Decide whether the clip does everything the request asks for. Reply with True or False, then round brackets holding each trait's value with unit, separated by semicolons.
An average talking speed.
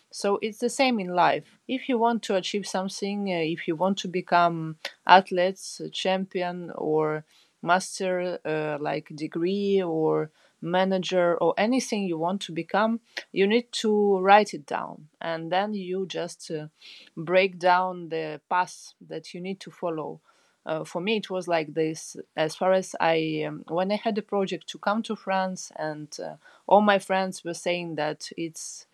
True (170 wpm)